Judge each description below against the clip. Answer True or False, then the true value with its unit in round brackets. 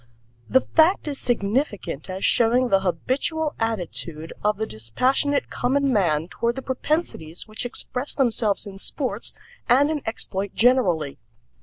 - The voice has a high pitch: True (230 Hz)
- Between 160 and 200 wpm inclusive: False (135 wpm)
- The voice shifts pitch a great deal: True (5.9 semitones)